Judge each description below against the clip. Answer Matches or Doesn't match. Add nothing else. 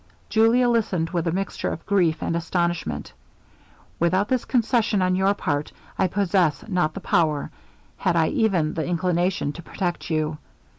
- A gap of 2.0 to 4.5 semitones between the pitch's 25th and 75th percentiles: Matches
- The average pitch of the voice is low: Doesn't match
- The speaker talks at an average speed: Matches